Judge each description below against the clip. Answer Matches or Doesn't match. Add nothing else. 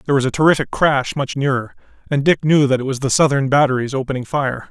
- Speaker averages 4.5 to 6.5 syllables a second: Matches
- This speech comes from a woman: Doesn't match